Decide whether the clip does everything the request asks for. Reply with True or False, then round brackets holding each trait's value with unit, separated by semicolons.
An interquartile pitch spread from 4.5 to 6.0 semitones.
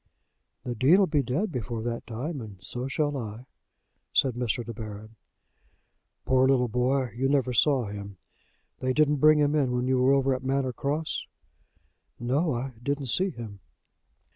False (3.0 semitones)